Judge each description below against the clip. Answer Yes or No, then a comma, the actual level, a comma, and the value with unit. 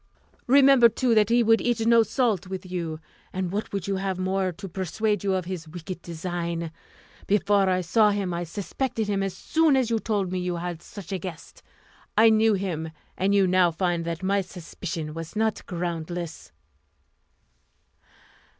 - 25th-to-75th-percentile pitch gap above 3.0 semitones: Yes, average, 3.5 semitones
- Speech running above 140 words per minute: Yes, average, 175 wpm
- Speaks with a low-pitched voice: No, high, 190 Hz